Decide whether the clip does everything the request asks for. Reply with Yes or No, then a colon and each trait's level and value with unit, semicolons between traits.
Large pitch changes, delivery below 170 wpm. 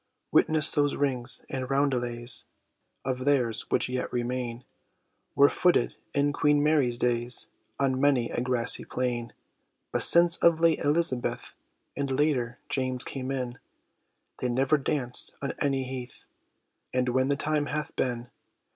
No: narrow, 2.6 semitones; average, 140 wpm